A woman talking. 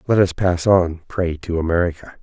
No: male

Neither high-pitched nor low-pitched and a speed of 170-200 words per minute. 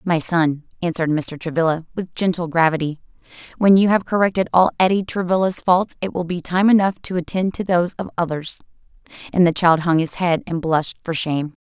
Yes: medium, 175 Hz; average, 190 wpm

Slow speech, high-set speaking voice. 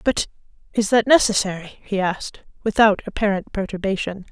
Yes: slow, 125 wpm; high, 205 Hz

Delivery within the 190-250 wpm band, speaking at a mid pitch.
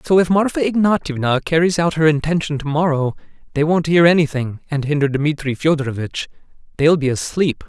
No: average, 165 wpm; medium, 155 Hz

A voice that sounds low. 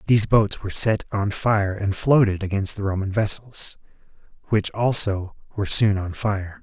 Yes: low, 105 Hz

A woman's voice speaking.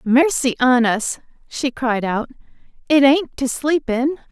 Yes: female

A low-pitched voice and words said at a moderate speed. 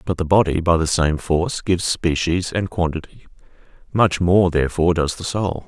Yes: very low, 85 Hz; average, 180 wpm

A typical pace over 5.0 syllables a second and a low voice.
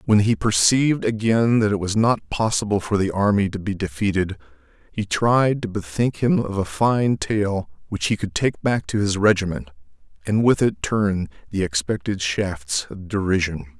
No: 4.7 syllables/s; low, 100 Hz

